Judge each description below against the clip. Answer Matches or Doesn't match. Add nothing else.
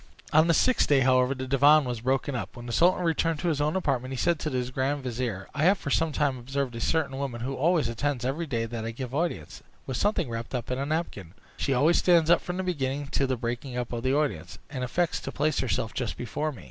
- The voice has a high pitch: Doesn't match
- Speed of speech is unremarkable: Doesn't match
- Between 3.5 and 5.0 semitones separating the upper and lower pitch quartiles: Matches